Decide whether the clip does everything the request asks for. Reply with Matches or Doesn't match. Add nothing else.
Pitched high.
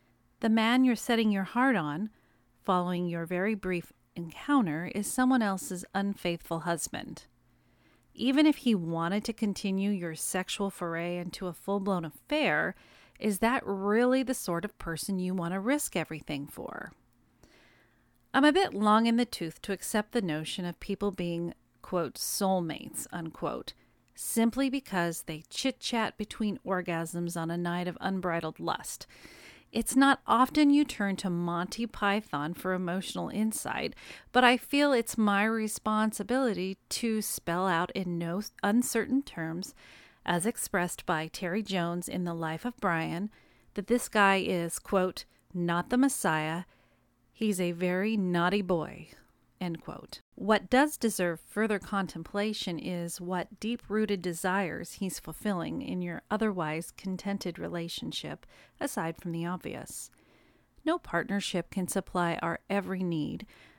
Matches